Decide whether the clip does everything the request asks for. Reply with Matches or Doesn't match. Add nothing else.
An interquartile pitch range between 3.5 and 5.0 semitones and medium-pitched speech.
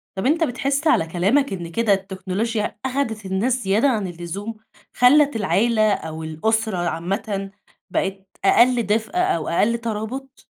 Doesn't match